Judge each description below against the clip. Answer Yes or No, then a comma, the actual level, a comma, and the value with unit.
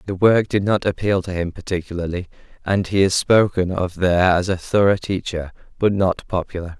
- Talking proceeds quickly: No, average, 185 wpm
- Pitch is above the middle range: No, very low, 95 Hz